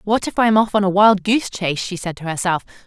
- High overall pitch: Yes, high, 195 Hz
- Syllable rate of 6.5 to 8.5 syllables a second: Yes, 6.7 syllables/s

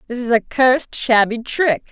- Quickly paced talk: No, average, 190 wpm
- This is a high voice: Yes, high, 240 Hz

